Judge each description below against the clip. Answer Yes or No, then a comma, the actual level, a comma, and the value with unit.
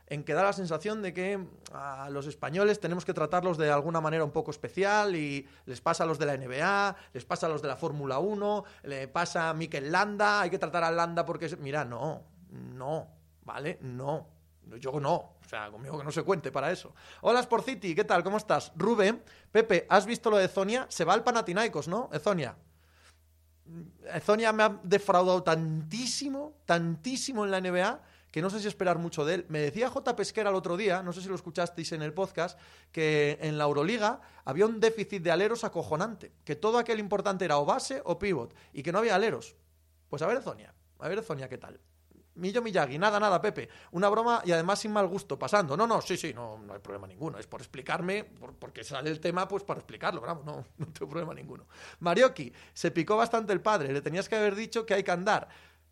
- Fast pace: Yes, fast, 215 wpm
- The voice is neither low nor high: Yes, medium, 175 Hz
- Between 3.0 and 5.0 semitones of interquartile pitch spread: No, wide, 5.6 semitones